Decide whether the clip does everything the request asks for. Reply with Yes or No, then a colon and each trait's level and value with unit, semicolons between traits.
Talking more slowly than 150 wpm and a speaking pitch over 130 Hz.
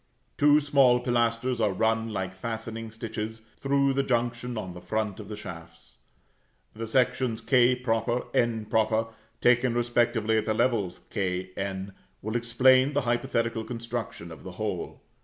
No: average, 140 wpm; low, 115 Hz